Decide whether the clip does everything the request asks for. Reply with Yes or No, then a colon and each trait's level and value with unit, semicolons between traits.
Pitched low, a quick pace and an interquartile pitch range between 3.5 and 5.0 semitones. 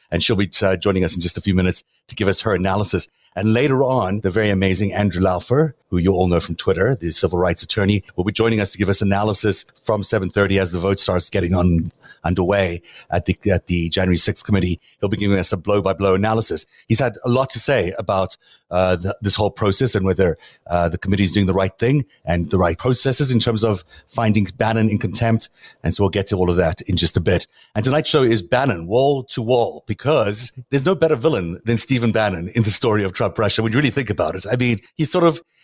Yes: low, 100 Hz; fast, 245 wpm; average, 3.8 semitones